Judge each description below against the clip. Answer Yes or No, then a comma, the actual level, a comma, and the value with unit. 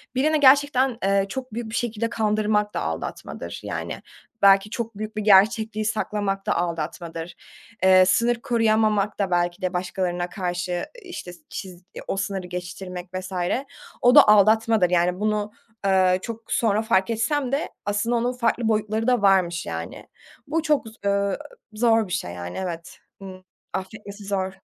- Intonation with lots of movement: No, average, 3.3 semitones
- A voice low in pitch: No, high, 205 Hz